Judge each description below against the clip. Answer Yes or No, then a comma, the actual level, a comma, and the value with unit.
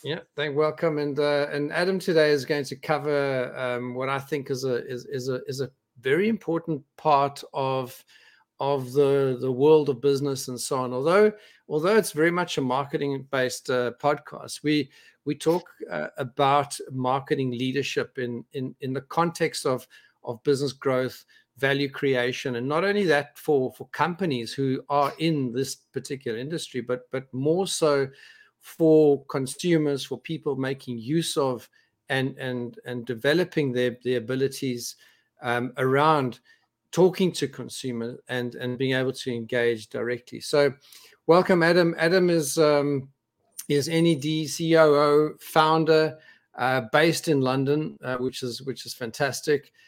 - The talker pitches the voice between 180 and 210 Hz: No, medium, 140 Hz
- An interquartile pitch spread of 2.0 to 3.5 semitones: Yes, average, 3.2 semitones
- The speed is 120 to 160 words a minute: Yes, average, 155 wpm